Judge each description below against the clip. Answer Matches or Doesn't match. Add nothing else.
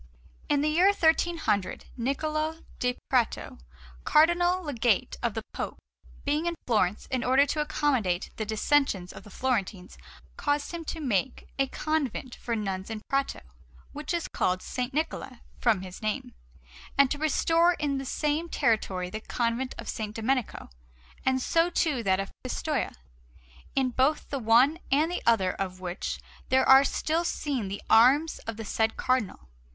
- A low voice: Doesn't match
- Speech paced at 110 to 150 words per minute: Doesn't match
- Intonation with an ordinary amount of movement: Doesn't match